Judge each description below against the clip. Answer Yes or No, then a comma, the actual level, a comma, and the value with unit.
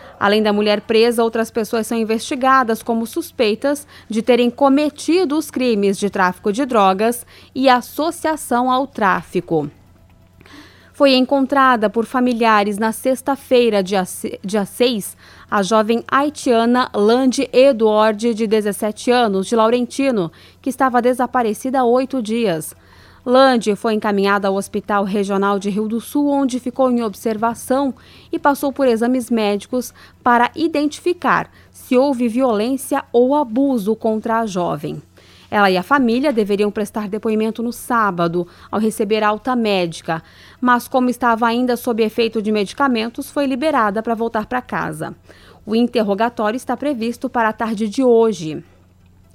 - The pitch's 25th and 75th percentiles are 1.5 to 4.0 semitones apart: Yes, average, 3.6 semitones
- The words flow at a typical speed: Yes, average, 135 wpm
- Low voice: No, high, 230 Hz